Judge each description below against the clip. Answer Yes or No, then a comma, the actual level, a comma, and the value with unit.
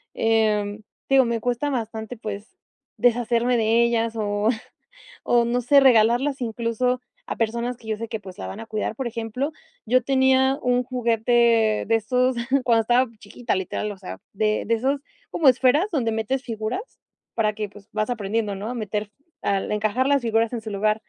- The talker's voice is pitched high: Yes, high, 230 Hz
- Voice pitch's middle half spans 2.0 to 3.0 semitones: Yes, narrow, 2.5 semitones